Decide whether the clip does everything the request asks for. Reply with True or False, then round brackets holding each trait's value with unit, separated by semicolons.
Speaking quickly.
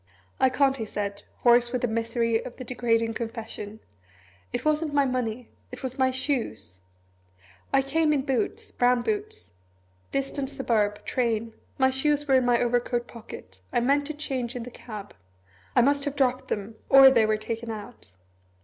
False (175 wpm)